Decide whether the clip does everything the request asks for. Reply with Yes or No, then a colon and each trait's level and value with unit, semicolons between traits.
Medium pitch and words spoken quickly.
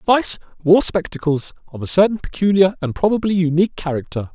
No: medium, 175 Hz; average, 150 wpm